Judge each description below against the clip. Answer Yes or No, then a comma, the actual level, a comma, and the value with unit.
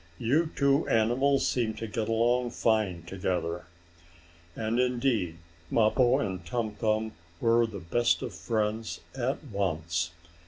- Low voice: Yes, low, 110 Hz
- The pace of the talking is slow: Yes, slow, 125 wpm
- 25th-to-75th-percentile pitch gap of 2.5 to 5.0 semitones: Yes, average, 3.7 semitones